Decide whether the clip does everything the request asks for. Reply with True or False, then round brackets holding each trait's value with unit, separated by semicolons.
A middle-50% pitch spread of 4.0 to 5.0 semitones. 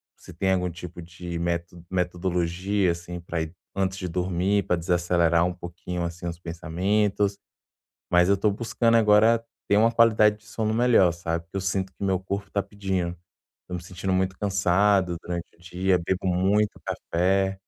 False (2.4 semitones)